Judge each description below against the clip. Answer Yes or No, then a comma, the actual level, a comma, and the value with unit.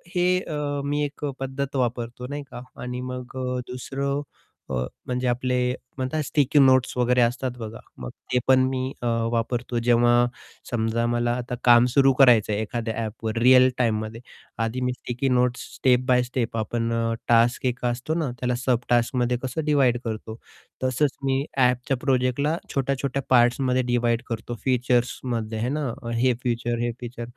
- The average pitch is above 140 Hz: No, low, 125 Hz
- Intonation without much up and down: Yes, narrow, 1.6 semitones